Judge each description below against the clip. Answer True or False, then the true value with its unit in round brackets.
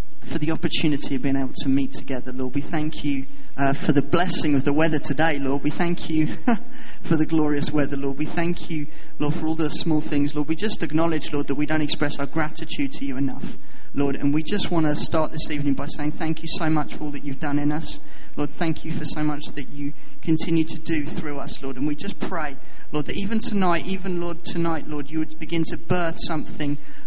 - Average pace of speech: False (240 wpm)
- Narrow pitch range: True (2.2 semitones)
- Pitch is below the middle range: False (155 Hz)